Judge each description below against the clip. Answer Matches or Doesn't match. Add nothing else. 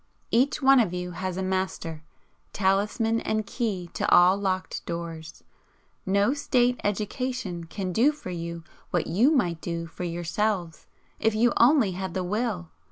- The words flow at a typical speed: Matches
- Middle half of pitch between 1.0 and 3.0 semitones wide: Doesn't match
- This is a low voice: Doesn't match